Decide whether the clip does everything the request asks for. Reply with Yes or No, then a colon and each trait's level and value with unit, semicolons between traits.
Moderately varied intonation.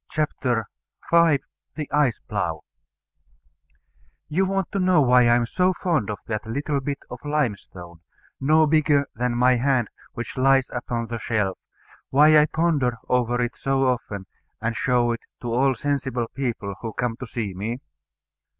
Yes: average, 4.0 semitones